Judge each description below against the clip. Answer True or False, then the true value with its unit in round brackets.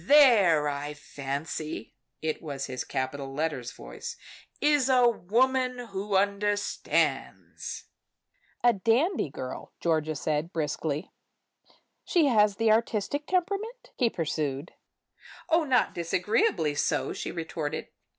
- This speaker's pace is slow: True (110 wpm)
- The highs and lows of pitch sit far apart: True (8.6 semitones)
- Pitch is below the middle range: False (185 Hz)